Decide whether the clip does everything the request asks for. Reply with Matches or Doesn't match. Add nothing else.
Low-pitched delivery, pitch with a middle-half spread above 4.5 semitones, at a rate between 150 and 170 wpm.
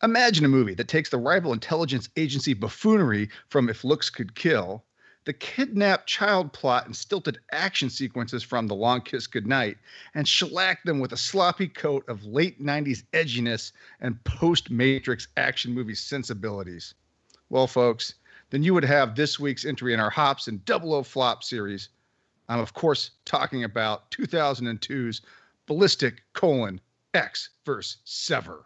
Matches